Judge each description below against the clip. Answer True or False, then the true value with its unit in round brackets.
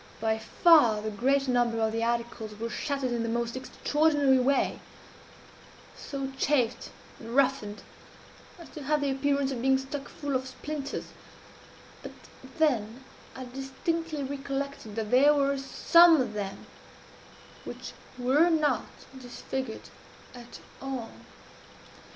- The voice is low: False (265 Hz)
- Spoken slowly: True (125 wpm)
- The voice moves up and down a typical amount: True (3.2 semitones)